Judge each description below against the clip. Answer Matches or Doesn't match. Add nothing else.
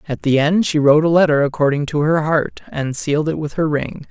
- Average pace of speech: Doesn't match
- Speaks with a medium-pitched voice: Matches